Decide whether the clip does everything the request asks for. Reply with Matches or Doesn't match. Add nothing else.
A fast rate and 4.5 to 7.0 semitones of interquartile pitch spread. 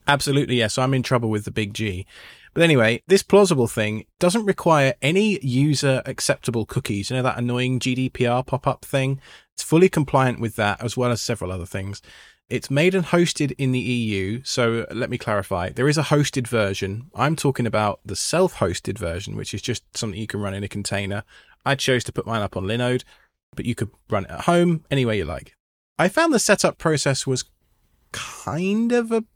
Matches